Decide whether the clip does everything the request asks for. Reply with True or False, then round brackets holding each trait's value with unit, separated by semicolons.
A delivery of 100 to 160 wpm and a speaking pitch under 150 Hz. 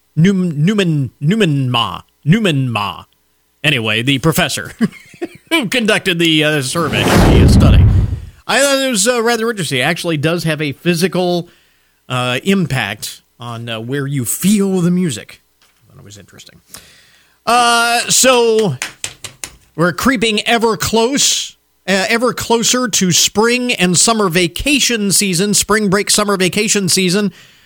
False (135 wpm; 180 Hz)